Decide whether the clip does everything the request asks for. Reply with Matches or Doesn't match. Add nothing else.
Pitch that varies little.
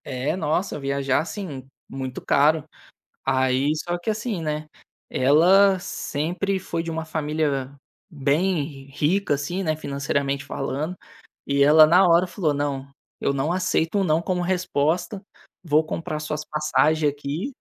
Doesn't match